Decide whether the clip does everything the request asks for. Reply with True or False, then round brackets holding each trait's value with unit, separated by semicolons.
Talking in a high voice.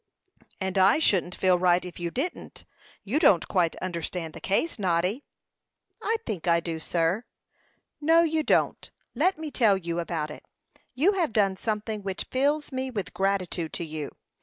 True (195 Hz)